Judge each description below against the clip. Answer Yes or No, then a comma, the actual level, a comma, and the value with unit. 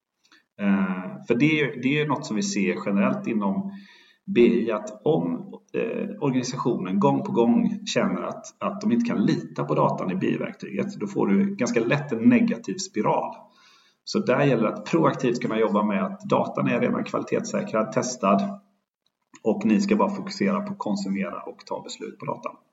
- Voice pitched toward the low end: No, high, 195 Hz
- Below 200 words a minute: Yes, average, 170 wpm